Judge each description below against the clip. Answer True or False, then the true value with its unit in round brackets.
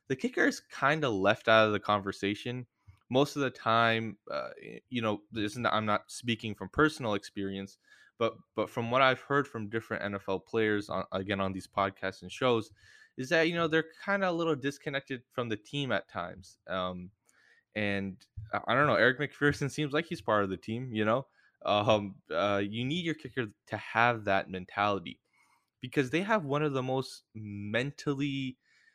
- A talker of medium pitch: False (115 Hz)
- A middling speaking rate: True (190 wpm)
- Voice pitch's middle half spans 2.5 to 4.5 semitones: False (5.3 semitones)